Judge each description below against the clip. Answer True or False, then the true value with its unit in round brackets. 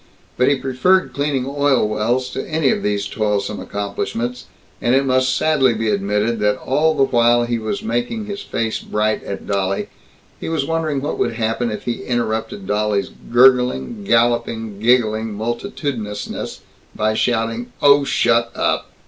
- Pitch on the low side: True (120 Hz)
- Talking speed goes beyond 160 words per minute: False (155 wpm)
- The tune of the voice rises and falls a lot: False (4.0 semitones)